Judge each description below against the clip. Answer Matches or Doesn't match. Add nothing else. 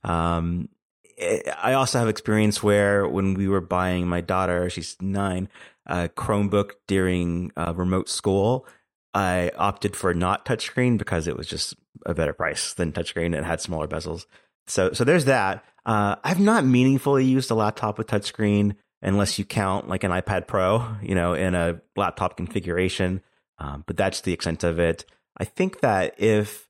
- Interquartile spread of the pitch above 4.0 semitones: Doesn't match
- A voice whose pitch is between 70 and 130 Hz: Matches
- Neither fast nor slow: Matches